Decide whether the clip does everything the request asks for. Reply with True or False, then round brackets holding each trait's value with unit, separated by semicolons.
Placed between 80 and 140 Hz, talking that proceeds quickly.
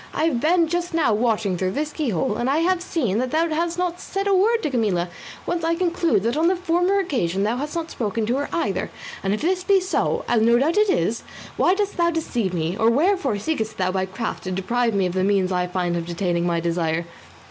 False (245 Hz; 245 wpm)